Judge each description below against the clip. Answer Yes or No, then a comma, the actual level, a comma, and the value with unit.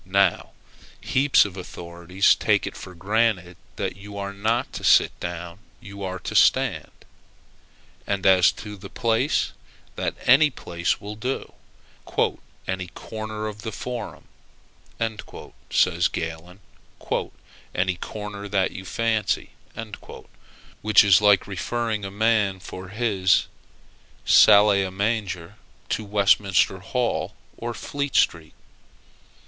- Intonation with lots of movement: No, average, 2.8 semitones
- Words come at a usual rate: No, slow, 120 wpm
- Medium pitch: No, low, 100 Hz